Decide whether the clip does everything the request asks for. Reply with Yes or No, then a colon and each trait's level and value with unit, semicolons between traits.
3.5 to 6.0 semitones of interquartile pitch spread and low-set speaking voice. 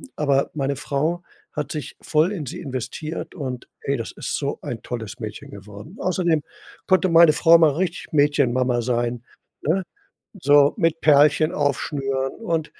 No: average, 4.0 semitones; medium, 145 Hz